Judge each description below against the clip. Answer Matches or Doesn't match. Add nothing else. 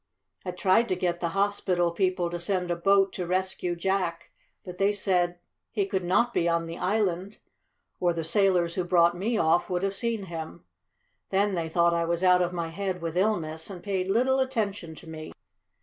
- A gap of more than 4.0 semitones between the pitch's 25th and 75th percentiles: Doesn't match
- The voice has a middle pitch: Matches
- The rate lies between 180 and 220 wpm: Matches